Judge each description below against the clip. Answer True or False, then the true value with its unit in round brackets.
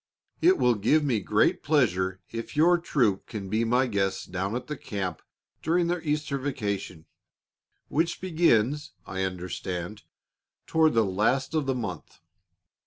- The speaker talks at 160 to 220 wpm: False (145 wpm)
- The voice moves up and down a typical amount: False (7.7 semitones)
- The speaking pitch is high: False (120 Hz)